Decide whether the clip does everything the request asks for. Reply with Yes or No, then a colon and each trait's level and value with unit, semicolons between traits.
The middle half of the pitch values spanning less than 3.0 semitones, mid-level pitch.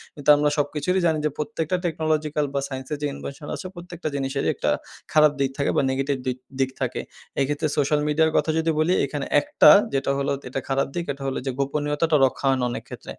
Yes: narrow, 2.5 semitones; medium, 145 Hz